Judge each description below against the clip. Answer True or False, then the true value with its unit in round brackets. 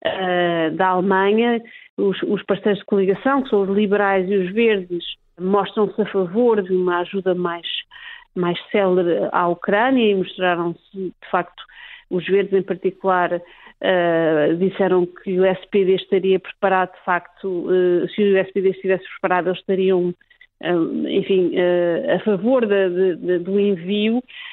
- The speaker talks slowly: False (145 wpm)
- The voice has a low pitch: False (190 Hz)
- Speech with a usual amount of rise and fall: False (2.1 semitones)